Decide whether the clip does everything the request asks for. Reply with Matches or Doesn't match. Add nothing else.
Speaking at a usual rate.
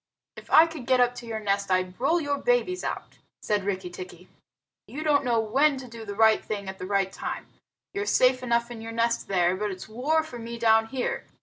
Doesn't match